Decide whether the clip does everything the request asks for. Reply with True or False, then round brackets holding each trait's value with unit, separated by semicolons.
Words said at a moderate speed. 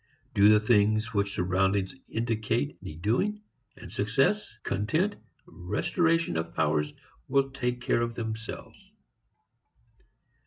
False (110 wpm)